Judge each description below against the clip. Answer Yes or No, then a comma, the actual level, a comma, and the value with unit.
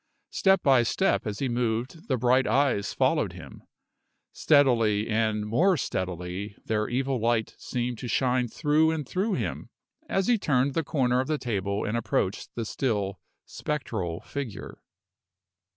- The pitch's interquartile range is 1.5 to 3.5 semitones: No, average, 4.8 semitones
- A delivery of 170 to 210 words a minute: No, average, 150 wpm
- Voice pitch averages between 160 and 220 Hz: No, low, 125 Hz